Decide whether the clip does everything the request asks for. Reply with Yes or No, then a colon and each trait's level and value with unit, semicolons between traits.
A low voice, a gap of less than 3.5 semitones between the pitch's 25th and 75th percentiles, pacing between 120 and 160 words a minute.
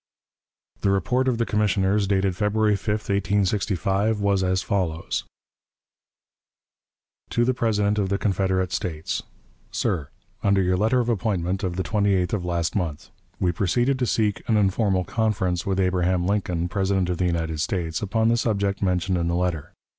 Yes: very low, 95 Hz; average, 2.7 semitones; average, 155 wpm